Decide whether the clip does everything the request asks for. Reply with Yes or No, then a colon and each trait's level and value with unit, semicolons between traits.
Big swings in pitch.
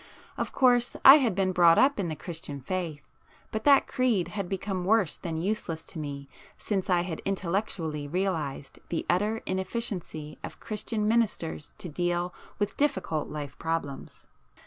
No: average, 4.7 semitones